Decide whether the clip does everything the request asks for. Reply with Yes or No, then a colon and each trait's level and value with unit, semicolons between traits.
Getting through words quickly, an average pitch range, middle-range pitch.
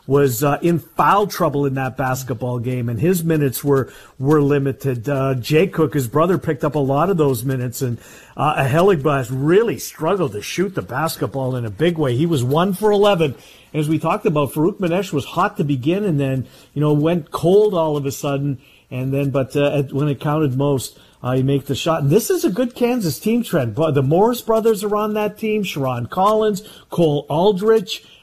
Yes: fast, 210 wpm; average, 4.8 semitones; medium, 150 Hz